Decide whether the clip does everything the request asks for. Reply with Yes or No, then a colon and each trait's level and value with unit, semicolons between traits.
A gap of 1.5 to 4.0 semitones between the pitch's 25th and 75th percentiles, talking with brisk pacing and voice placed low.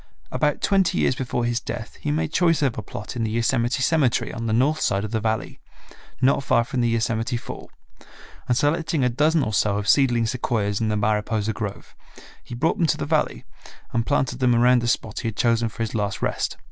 Yes: average, 3.4 semitones; fast, 220 wpm; low, 120 Hz